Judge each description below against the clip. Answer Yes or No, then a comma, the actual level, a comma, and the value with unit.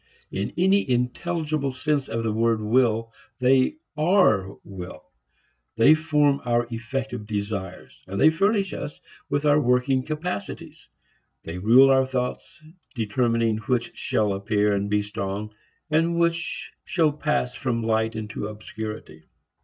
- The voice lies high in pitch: No, low, 120 Hz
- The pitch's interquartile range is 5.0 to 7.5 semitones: Yes, wide, 5.6 semitones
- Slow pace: Yes, slow, 130 wpm